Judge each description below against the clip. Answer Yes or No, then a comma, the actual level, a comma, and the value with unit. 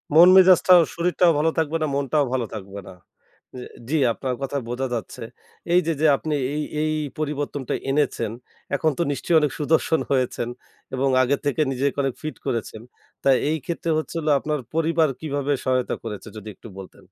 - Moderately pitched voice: Yes, medium, 145 Hz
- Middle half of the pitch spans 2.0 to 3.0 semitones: No, average, 3.6 semitones